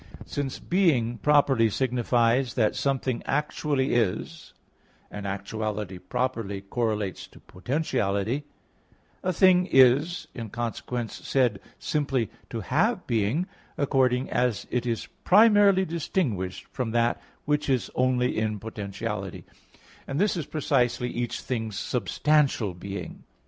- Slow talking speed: Yes, slow, 115 wpm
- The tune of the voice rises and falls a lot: No, average, 4.7 semitones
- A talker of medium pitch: No, low, 125 Hz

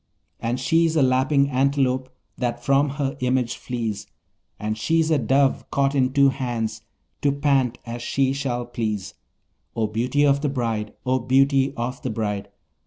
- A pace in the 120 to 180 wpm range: Yes, average, 160 wpm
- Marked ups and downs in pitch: No, average, 2.8 semitones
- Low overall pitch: Yes, low, 130 Hz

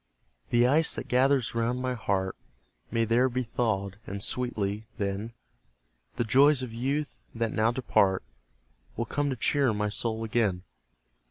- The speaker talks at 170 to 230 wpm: No, average, 150 wpm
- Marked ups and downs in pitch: No, average, 3.2 semitones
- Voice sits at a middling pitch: No, low, 115 Hz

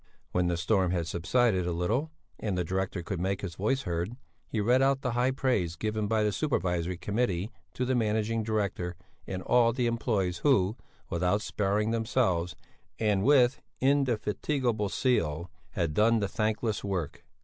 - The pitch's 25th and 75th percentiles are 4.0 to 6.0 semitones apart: Yes, average, 5.0 semitones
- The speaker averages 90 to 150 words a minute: No, average, 160 wpm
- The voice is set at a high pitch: No, low, 105 Hz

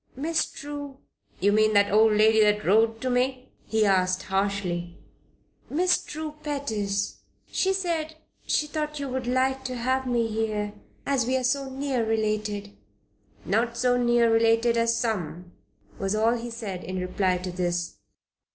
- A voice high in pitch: Yes, high, 225 Hz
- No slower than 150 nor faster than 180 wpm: Yes, average, 160 wpm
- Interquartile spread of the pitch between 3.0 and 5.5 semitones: Yes, average, 4.3 semitones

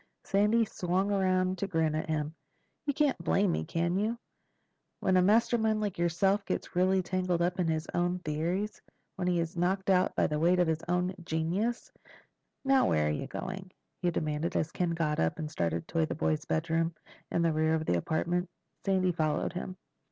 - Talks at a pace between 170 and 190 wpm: Yes, average, 185 wpm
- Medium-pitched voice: Yes, medium, 175 Hz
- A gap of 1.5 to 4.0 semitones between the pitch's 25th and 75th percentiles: Yes, average, 3.0 semitones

